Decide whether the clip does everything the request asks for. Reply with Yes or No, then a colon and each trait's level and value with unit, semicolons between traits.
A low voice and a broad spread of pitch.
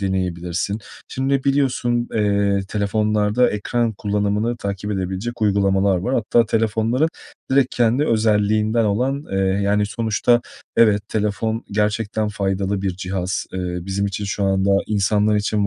No: low, 105 Hz; narrow, 2.4 semitones